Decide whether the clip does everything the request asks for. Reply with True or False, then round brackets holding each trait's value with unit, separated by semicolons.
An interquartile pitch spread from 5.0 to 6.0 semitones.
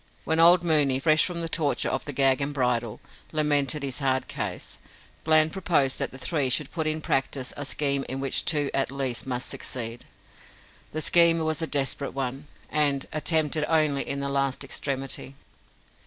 False (2.5 semitones)